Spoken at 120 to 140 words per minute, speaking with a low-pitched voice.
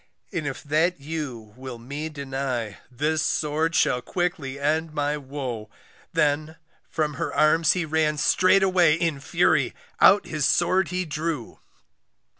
No: slow, 135 wpm; medium, 150 Hz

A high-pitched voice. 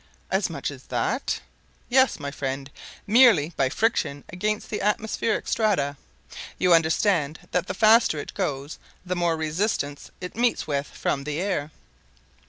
No: medium, 175 Hz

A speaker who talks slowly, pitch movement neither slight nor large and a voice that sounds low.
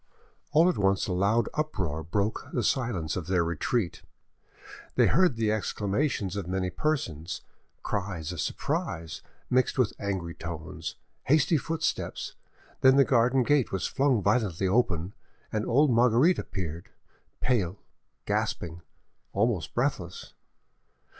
No: slow, 125 wpm; wide, 6.1 semitones; low, 105 Hz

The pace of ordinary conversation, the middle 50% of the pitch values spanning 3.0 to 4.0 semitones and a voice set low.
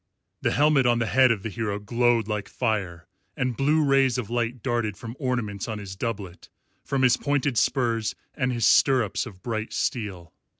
Yes: average, 180 wpm; average, 3.4 semitones; low, 115 Hz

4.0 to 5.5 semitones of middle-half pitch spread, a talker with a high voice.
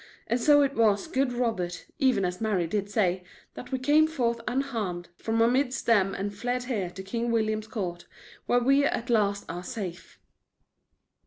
Yes: average, 4.3 semitones; high, 225 Hz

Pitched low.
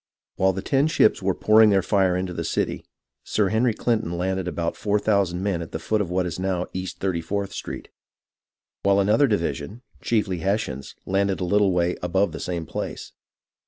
Yes: very low, 95 Hz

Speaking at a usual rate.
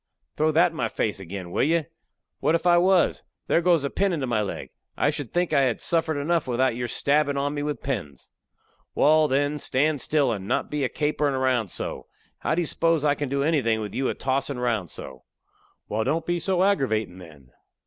No: fast, 215 wpm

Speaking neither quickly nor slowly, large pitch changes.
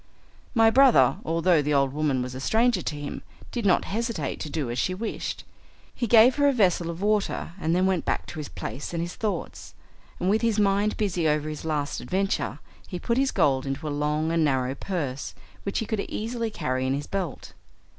No: fast, 210 wpm; wide, 6.3 semitones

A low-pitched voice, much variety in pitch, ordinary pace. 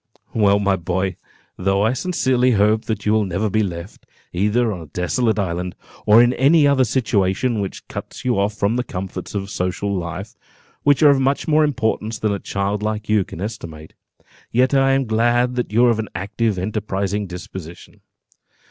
No: low, 105 Hz; average, 4.0 semitones; average, 185 wpm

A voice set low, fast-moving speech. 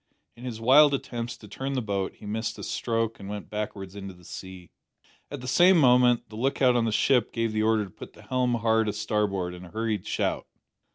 Yes: low, 115 Hz; fast, 225 wpm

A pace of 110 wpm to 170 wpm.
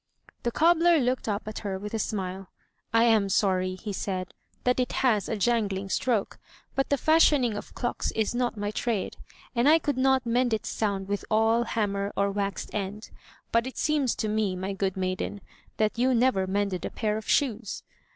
No: average, 190 wpm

